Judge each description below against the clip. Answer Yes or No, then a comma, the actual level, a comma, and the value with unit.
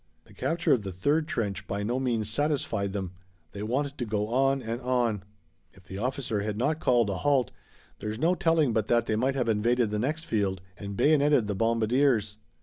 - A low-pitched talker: Yes, low, 115 Hz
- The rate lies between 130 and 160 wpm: No, average, 200 wpm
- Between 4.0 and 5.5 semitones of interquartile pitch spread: Yes, average, 4.6 semitones